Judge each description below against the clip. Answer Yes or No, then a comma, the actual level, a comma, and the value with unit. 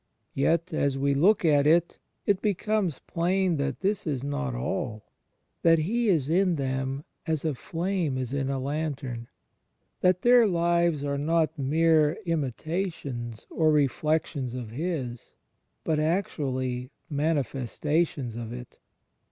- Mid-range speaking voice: Yes, medium, 150 Hz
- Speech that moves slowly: Yes, slow, 130 wpm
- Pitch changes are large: No, average, 4.2 semitones